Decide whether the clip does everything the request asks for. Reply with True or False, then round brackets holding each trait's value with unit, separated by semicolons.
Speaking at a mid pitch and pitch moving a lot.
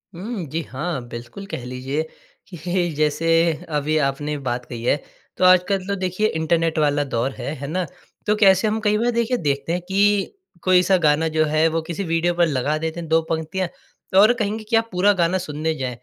False (165 Hz; 4.3 semitones)